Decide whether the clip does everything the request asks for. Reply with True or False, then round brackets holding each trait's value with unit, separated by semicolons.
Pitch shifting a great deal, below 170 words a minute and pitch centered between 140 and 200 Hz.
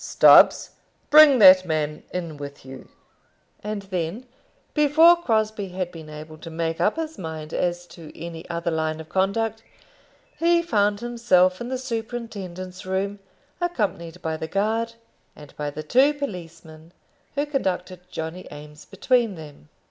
True (6.0 semitones; 145 wpm; 185 Hz)